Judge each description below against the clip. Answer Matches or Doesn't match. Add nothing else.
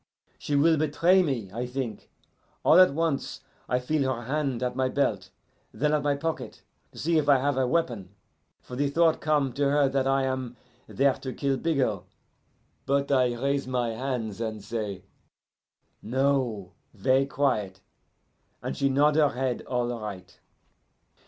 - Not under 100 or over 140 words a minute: Doesn't match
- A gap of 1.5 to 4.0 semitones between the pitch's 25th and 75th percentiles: Matches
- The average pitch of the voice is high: Doesn't match